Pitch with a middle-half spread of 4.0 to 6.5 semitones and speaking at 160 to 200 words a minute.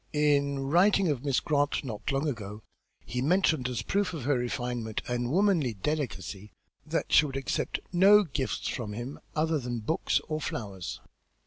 Yes: average, 4.6 semitones; average, 165 wpm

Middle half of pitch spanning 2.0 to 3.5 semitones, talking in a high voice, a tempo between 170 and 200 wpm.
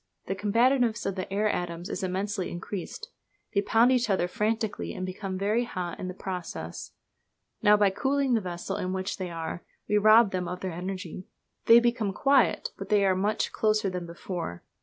Yes: average, 3.0 semitones; high, 195 Hz; average, 185 wpm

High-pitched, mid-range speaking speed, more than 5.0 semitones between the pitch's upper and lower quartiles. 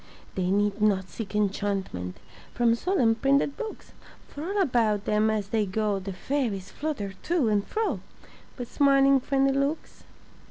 Yes: high, 225 Hz; average, 150 wpm; wide, 5.4 semitones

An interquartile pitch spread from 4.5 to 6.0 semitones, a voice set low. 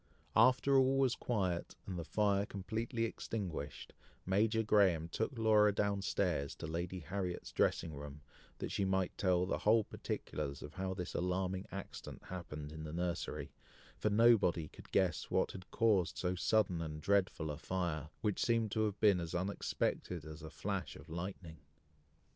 No: average, 3.9 semitones; very low, 95 Hz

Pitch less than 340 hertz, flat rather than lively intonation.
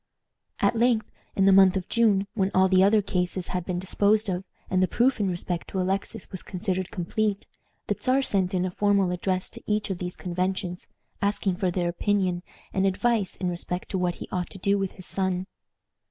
Yes: high, 190 Hz; narrow, 1.9 semitones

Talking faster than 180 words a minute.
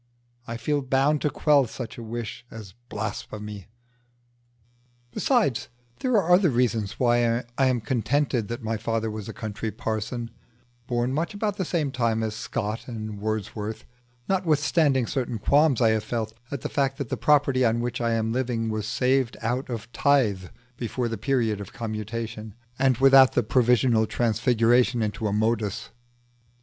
No: average, 160 wpm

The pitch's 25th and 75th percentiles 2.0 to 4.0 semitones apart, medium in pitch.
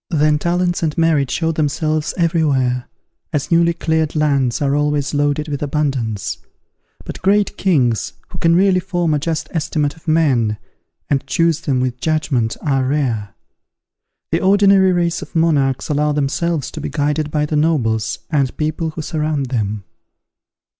Yes: average, 3.2 semitones; medium, 150 Hz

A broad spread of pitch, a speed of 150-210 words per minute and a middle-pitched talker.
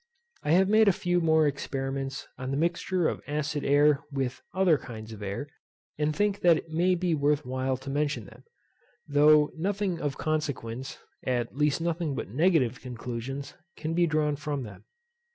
No: average, 3.6 semitones; average, 170 wpm; medium, 150 Hz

